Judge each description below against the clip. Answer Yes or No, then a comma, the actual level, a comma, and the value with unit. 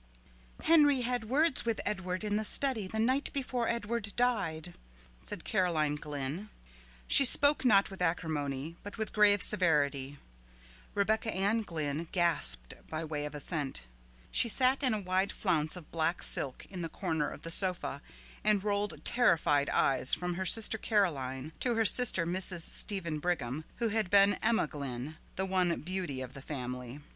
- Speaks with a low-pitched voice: No, medium, 180 Hz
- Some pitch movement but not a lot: No, wide, 6.3 semitones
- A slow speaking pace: No, average, 160 wpm